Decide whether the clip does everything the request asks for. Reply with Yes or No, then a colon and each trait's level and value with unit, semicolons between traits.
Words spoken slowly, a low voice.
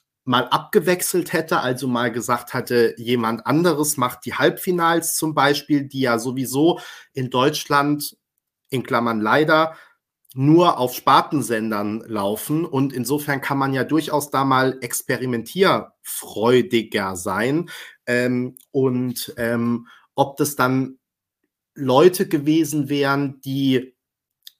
Yes: slow, 110 wpm; low, 130 Hz